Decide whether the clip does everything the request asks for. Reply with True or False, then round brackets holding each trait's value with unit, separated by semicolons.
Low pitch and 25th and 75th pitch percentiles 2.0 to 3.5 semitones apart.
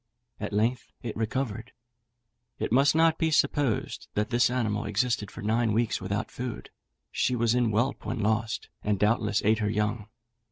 True (115 Hz; 2.8 semitones)